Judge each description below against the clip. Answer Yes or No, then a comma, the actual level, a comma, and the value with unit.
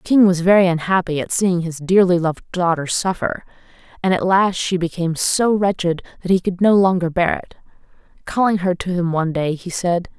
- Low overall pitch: No, medium, 180 Hz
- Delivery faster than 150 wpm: Yes, average, 200 wpm